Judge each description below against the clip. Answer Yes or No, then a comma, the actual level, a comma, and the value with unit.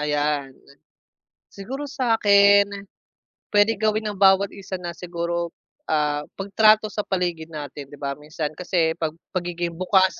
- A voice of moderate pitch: Yes, medium, 180 Hz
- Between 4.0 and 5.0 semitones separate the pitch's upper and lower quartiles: Yes, average, 4.4 semitones